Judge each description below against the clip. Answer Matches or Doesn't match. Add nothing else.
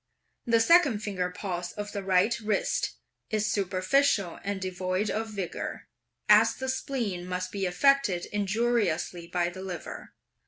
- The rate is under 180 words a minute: Matches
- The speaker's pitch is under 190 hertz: Doesn't match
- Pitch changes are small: Doesn't match